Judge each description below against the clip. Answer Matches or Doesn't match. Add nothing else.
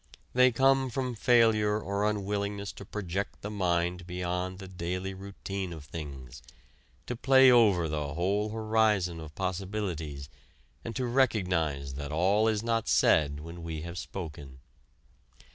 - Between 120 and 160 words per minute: Matches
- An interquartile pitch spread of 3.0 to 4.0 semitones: Doesn't match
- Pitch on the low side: Matches